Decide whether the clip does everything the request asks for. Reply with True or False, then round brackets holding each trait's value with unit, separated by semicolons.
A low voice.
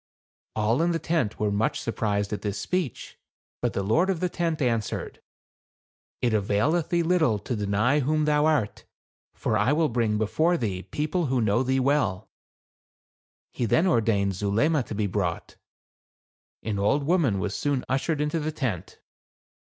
True (125 Hz)